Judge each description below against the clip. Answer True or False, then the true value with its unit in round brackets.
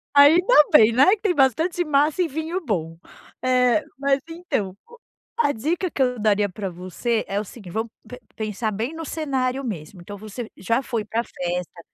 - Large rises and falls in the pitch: True (6.6 semitones)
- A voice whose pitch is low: False (250 Hz)